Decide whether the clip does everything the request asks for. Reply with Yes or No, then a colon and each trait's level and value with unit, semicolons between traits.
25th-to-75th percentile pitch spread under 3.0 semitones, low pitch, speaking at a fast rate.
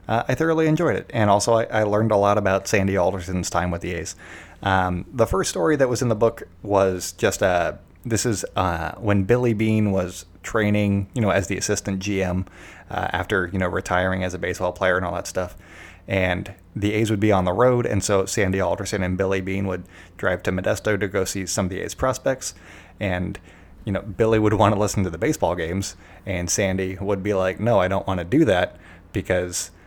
Yes: narrow, 2.6 semitones; very low, 95 Hz; fast, 225 wpm